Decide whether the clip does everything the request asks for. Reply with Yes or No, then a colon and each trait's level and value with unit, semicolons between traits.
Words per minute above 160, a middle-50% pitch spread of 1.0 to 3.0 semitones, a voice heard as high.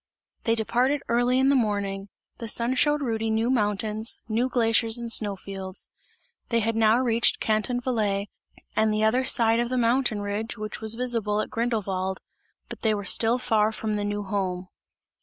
Yes: average, 175 wpm; narrow, 2.4 semitones; high, 225 Hz